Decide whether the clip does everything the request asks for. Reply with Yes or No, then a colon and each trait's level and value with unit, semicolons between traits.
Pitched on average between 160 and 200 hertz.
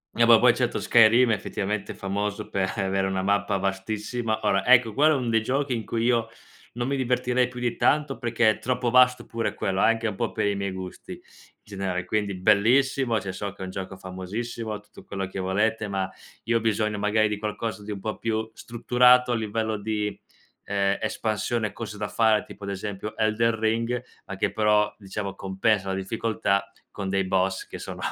No: low, 110 Hz